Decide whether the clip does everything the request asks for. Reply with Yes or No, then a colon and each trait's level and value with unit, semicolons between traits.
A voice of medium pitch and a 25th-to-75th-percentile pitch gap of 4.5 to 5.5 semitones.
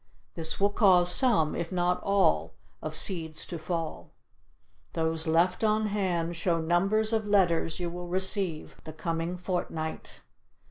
No: medium, 175 Hz; average, 3.0 semitones